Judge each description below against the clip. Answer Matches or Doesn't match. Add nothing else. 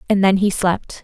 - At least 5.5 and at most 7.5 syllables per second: Doesn't match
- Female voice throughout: Matches